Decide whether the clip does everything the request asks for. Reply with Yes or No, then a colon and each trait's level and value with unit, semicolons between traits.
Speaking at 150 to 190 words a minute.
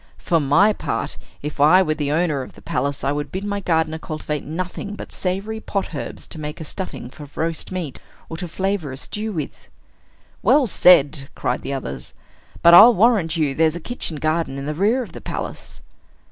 No: average, 200 wpm